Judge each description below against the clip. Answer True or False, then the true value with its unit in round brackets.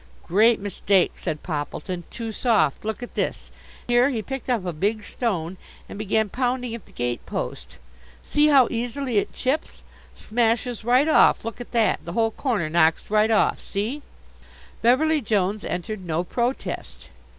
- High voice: True (220 Hz)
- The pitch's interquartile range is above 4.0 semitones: True (4.4 semitones)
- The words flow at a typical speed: True (160 wpm)